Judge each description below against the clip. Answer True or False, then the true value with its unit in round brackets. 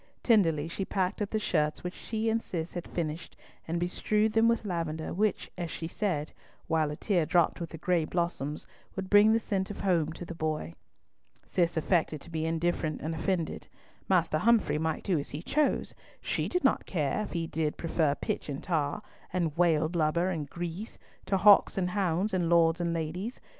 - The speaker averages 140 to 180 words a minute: False (195 wpm)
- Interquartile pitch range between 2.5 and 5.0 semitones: True (3.4 semitones)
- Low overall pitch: False (170 Hz)